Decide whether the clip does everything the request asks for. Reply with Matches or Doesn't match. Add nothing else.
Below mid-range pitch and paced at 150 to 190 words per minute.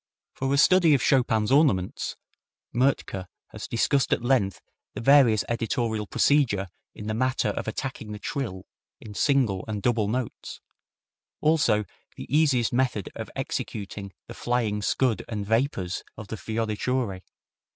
Doesn't match